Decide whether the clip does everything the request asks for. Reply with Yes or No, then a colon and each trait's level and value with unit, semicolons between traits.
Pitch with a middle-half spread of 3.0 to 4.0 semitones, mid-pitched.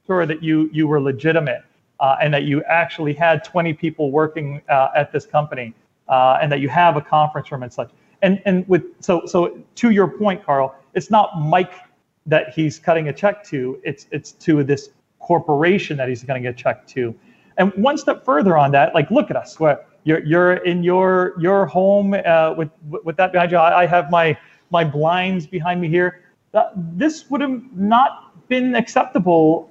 Yes: average, 3.7 semitones; medium, 165 Hz